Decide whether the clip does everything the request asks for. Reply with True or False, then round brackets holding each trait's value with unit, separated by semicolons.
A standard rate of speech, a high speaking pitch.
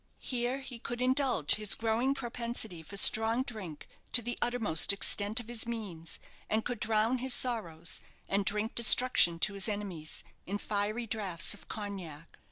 True (160 wpm; 220 Hz)